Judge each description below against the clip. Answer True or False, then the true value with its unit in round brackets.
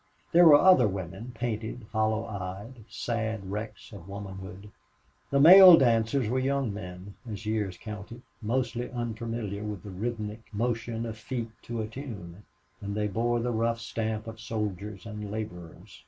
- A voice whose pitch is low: True (110 Hz)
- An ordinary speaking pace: True (155 wpm)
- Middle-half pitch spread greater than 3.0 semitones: False (2.5 semitones)